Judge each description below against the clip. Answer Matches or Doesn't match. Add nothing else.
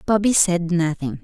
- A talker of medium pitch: Matches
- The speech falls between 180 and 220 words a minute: Doesn't match